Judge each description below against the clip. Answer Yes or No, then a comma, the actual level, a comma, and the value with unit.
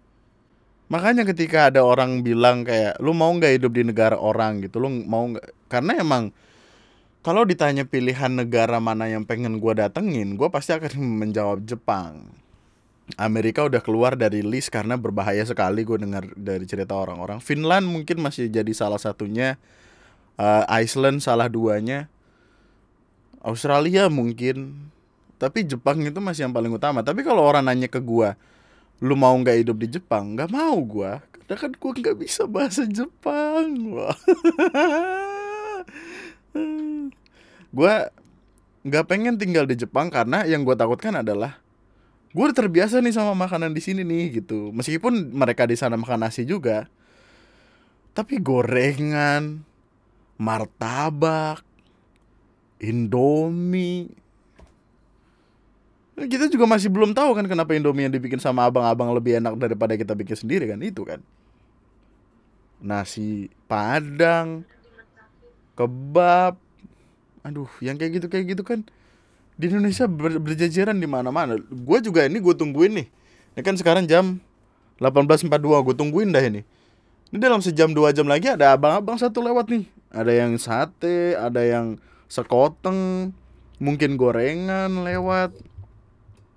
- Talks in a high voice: No, low, 135 Hz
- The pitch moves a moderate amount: No, wide, 7.7 semitones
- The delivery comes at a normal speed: Yes, average, 130 wpm